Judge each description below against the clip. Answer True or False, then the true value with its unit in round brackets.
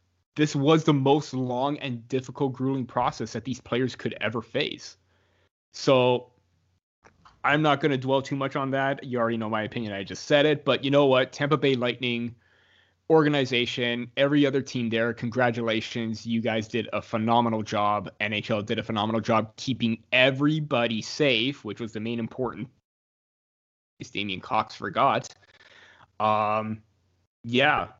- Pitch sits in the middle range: False (120 Hz)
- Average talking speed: True (155 wpm)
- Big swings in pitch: False (3.6 semitones)